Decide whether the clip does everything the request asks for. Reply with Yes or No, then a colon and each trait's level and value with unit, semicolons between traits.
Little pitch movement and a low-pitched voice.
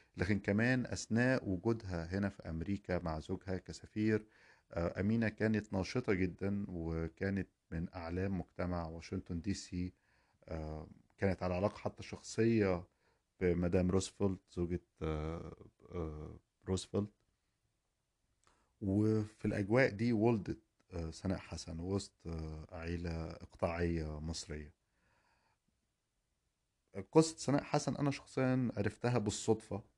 No: average, 3.9 semitones; very low, 95 Hz